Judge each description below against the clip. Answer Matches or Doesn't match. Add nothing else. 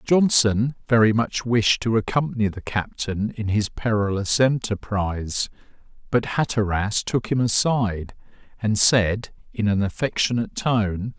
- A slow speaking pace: Matches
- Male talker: Matches